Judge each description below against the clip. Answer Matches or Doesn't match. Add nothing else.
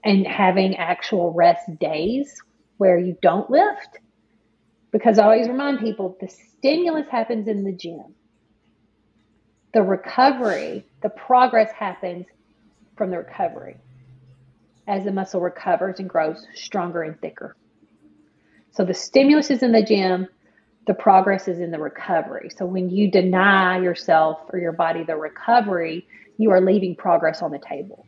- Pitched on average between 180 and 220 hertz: Matches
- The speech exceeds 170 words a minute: Doesn't match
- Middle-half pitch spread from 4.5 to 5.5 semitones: Doesn't match